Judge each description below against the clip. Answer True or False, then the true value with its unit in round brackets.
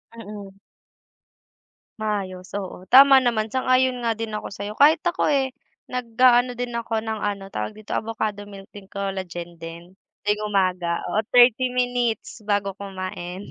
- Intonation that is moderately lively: True (4.0 semitones)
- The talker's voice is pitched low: False (215 Hz)